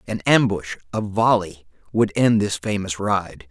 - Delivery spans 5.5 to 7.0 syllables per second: No, 4.1 syllables/s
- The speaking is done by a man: Yes, male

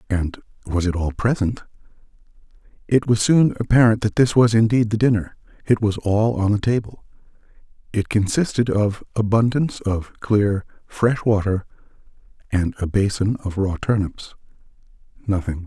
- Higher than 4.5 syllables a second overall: Yes, 5.0 syllables/s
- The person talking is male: Yes, male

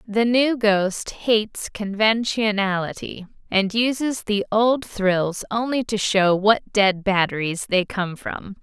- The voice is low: No, high, 210 Hz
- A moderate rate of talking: No, slow, 130 wpm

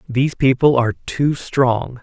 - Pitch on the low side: Yes, low, 130 Hz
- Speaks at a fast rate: No, average, 150 wpm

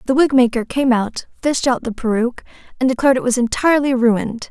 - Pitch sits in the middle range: No, very high, 250 Hz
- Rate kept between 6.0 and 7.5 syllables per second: Yes, 6.2 syllables/s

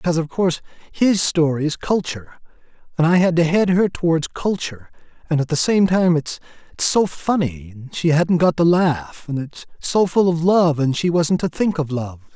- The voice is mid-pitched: Yes, medium, 165 Hz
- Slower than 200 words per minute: No, fast, 205 wpm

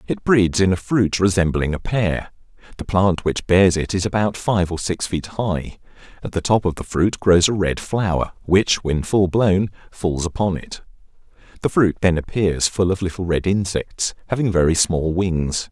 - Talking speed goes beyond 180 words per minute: Yes, average, 190 wpm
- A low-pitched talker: Yes, very low, 95 Hz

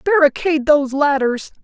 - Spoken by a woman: Yes, female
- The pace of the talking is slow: Yes, slow, 110 wpm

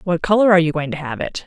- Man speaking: No, female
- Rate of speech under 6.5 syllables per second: No, 7.3 syllables/s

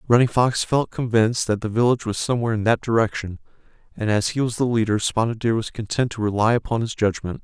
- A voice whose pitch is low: Yes, low, 115 Hz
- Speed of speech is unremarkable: No, fast, 220 wpm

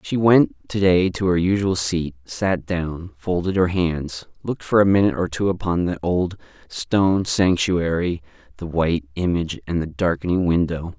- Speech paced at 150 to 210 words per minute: Yes, average, 170 wpm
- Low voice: Yes, very low, 85 Hz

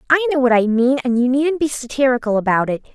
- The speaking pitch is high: Yes, very high, 255 Hz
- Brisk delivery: Yes, fast, 245 wpm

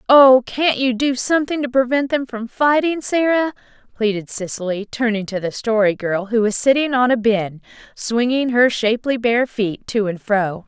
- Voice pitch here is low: No, high, 240 Hz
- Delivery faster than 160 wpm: Yes, average, 180 wpm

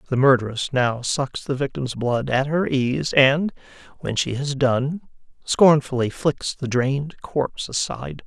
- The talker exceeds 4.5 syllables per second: No, 4.3 syllables/s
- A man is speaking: Yes, male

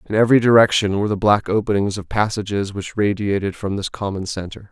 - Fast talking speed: No, average, 190 wpm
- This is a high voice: No, low, 100 Hz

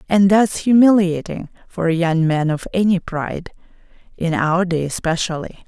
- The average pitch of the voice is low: No, medium, 175 Hz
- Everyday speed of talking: Yes, average, 150 wpm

